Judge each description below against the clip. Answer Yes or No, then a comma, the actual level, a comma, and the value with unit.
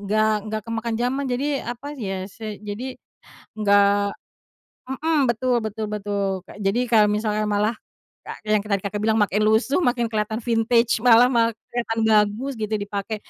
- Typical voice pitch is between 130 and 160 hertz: No, high, 220 Hz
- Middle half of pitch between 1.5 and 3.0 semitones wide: Yes, narrow, 2.5 semitones